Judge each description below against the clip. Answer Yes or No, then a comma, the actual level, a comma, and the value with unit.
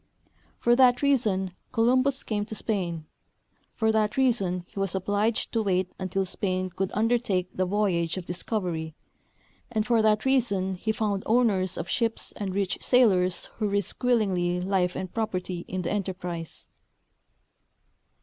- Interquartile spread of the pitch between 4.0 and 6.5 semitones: No, average, 3.5 semitones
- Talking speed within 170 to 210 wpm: No, average, 150 wpm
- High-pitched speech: Yes, high, 200 Hz